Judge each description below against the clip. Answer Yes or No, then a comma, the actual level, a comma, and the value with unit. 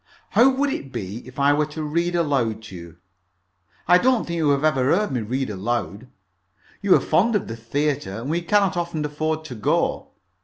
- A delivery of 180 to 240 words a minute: Yes, average, 200 wpm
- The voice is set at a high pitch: No, medium, 145 Hz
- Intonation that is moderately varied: No, wide, 6.2 semitones